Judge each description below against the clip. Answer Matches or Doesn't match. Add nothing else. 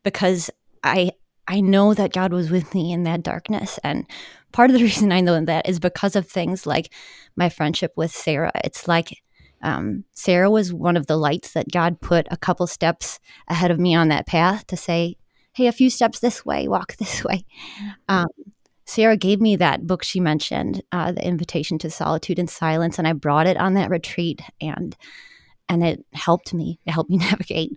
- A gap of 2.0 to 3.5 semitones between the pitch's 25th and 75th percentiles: Matches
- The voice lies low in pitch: Doesn't match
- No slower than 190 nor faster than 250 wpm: Matches